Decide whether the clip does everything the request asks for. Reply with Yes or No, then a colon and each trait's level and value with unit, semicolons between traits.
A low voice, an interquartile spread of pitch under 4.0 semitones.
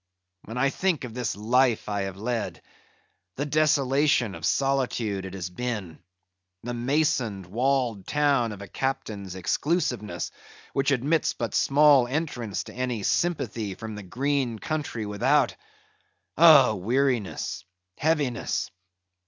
No: low, 125 Hz; average, 4.9 semitones